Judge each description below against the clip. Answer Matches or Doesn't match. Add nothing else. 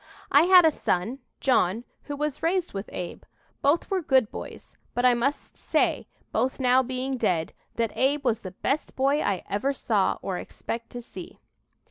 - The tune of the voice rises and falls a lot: Doesn't match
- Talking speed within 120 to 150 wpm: Doesn't match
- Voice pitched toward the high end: Matches